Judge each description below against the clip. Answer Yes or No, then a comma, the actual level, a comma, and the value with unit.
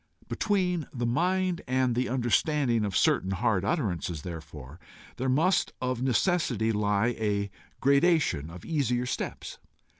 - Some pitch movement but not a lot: No, wide, 6.8 semitones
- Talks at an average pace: No, slow, 125 wpm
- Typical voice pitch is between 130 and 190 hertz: No, low, 120 Hz